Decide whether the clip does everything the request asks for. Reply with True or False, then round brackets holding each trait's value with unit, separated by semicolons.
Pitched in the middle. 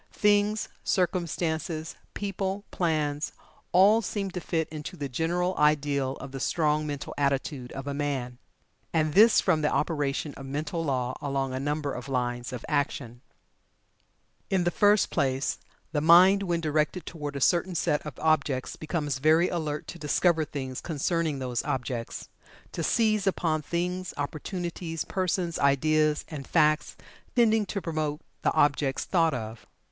True (155 Hz)